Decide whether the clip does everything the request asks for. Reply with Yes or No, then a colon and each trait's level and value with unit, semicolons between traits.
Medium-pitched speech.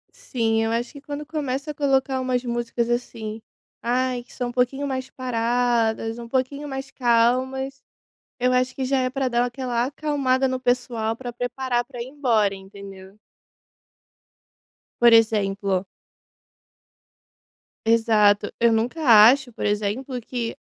No: high, 245 Hz